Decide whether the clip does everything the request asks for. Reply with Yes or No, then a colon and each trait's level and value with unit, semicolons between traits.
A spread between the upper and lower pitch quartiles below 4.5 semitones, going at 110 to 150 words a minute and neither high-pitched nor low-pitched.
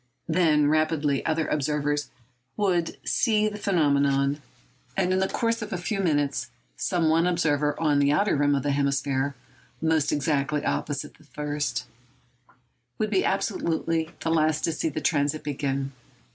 Yes: average, 2.8 semitones; average, 145 wpm; medium, 150 Hz